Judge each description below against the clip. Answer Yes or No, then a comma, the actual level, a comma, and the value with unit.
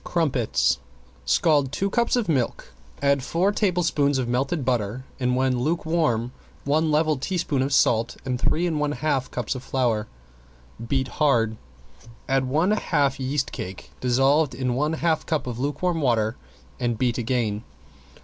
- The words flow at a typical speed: Yes, average, 150 wpm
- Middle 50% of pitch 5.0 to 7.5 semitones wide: No, average, 4.0 semitones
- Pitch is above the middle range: No, low, 135 Hz